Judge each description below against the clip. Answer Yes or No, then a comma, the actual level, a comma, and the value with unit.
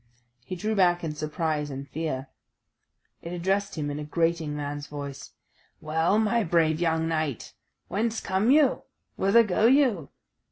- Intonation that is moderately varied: Yes, average, 4.9 semitones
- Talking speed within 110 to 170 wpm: Yes, average, 150 wpm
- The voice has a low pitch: No, medium, 165 Hz